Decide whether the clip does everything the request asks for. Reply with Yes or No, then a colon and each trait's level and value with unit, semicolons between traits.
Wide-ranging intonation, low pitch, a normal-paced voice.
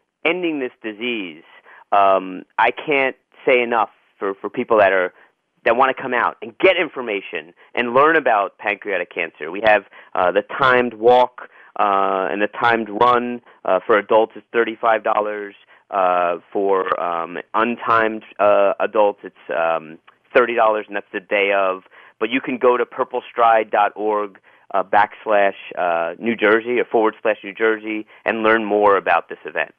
No: average, 3.4 semitones; low, 110 Hz; average, 160 wpm